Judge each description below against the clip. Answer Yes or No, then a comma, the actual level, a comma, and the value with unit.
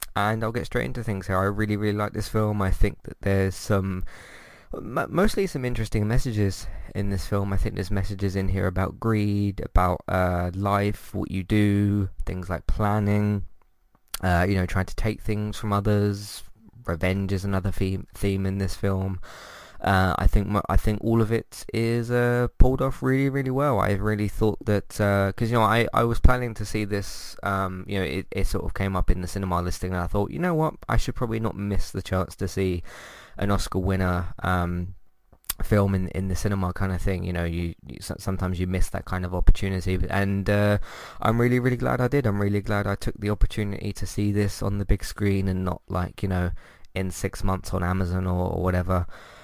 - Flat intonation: Yes, narrow, 2.3 semitones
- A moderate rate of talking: No, fast, 215 wpm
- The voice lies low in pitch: Yes, low, 100 Hz